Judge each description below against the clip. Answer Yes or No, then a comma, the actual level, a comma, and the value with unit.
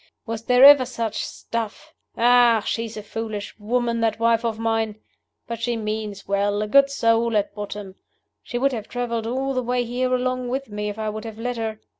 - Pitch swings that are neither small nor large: No, narrow, 2.3 semitones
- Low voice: No, high, 230 Hz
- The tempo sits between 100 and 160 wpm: No, average, 200 wpm